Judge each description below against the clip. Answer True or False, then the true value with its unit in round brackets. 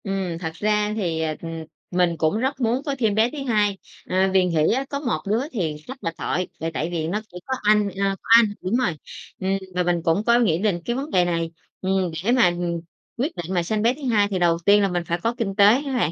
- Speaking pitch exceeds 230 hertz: False (195 Hz)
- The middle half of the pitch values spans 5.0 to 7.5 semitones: False (4.6 semitones)